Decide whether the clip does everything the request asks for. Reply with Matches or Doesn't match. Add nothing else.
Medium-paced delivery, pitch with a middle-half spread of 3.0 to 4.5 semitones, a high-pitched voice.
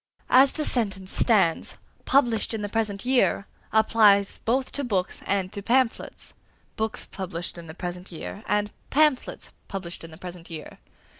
Matches